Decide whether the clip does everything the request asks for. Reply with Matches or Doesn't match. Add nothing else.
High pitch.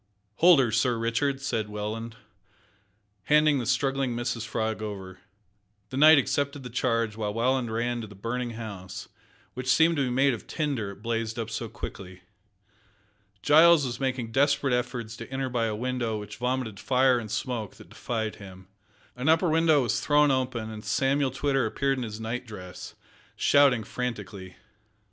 Doesn't match